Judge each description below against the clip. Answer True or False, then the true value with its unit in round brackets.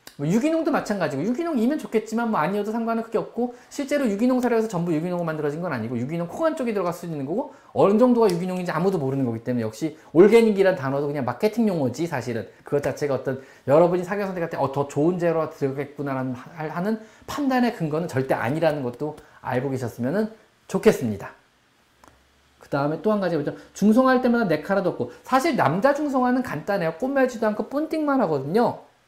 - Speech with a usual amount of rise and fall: False (8.0 semitones)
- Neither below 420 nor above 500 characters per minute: True (440 characters per minute)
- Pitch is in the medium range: True (180 Hz)